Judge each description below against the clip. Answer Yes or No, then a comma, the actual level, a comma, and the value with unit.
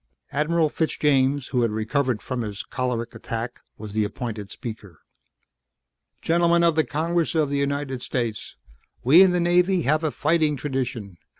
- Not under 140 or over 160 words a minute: Yes, average, 155 wpm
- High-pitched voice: No, medium, 140 Hz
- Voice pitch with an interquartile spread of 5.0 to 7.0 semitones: Yes, average, 5.3 semitones